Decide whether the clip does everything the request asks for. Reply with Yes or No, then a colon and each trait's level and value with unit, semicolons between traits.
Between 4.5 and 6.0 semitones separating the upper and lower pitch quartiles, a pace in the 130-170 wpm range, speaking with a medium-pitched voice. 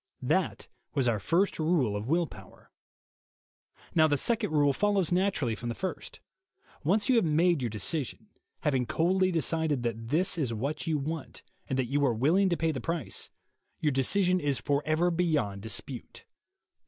Yes: average, 5.2 semitones; average, 165 wpm; medium, 155 Hz